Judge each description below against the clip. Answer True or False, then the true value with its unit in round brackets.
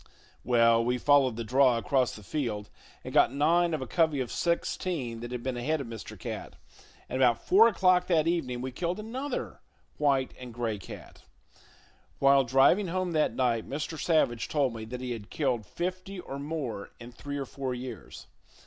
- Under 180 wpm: False (185 wpm)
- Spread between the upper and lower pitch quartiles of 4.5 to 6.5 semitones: True (5.2 semitones)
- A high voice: False (135 Hz)